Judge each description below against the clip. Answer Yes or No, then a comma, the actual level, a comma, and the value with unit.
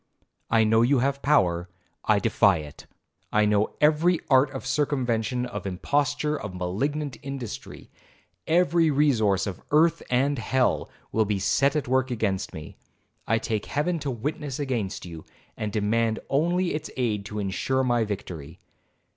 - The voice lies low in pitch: Yes, low, 120 Hz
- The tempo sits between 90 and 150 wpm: Yes, average, 145 wpm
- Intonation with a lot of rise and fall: Yes, wide, 5.7 semitones